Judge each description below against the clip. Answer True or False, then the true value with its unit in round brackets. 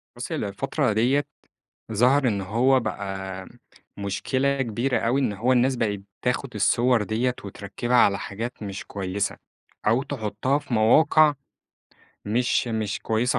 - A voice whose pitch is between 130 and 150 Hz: False (120 Hz)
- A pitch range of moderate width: True (3.9 semitones)